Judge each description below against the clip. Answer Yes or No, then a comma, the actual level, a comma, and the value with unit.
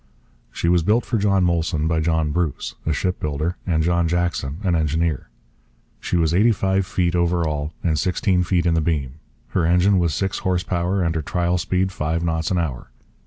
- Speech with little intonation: Yes, narrow, 2.2 semitones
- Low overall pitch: Yes, very low, 85 Hz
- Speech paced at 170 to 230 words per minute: Yes, average, 195 wpm